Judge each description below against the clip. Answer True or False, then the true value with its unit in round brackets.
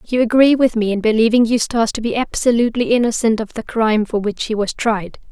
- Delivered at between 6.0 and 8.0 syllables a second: True (6.1 syllables/s)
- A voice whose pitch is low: False (225 Hz)